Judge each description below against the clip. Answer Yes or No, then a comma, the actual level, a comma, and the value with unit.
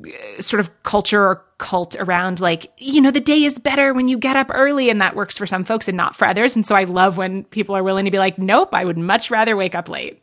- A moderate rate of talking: No, fast, 275 wpm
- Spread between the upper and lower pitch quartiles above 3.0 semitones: Yes, average, 5.3 semitones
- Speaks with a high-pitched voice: Yes, high, 205 Hz